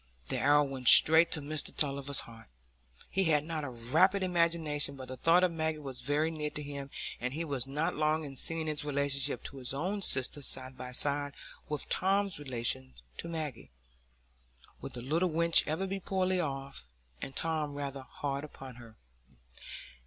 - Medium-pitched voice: Yes, medium, 145 Hz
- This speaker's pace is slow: No, average, 175 wpm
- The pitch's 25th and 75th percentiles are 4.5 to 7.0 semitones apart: No, average, 3.2 semitones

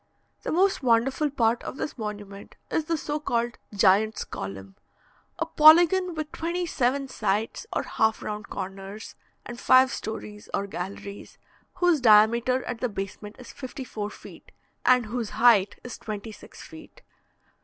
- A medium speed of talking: Yes, average, 150 wpm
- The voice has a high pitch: Yes, high, 235 Hz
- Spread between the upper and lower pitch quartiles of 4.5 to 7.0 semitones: Yes, average, 5.2 semitones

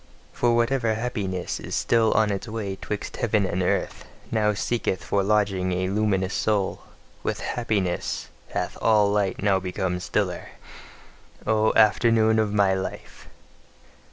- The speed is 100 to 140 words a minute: Yes, slow, 135 wpm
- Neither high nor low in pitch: No, low, 105 Hz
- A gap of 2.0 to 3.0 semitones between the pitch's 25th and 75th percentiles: Yes, narrow, 2.6 semitones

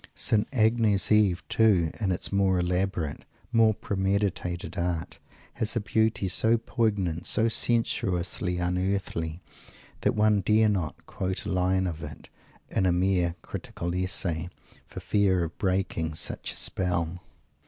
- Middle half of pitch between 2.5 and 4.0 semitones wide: Yes, average, 3.1 semitones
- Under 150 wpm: Yes, slow, 135 wpm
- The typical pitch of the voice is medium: No, very low, 95 Hz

